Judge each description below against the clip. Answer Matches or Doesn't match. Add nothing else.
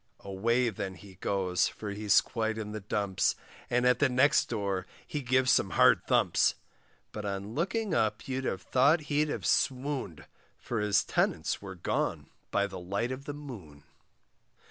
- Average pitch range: Matches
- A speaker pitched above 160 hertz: Doesn't match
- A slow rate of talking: Doesn't match